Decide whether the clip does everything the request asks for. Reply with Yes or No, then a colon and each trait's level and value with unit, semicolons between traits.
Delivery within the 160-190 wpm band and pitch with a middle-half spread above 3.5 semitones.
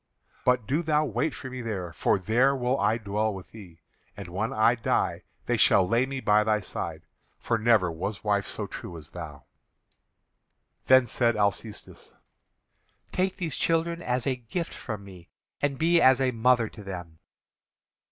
Yes: average, 170 wpm; average, 4.7 semitones